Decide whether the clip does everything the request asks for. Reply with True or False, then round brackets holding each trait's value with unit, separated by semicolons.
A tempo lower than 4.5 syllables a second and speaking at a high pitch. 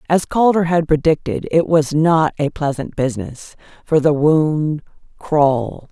False (4.2 syllables/s; 155 Hz)